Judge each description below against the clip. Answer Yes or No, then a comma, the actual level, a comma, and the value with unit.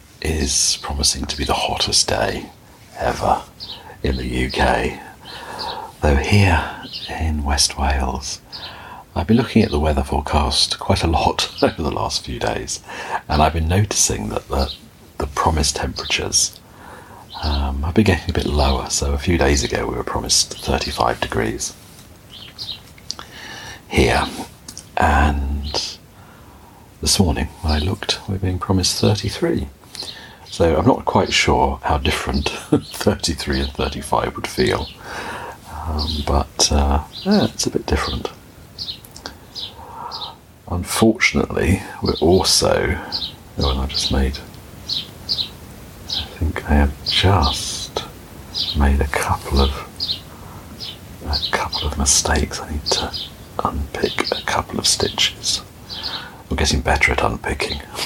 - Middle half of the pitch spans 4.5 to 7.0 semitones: Yes, average, 4.9 semitones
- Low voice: Yes, very low, 80 Hz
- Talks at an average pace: No, slow, 125 wpm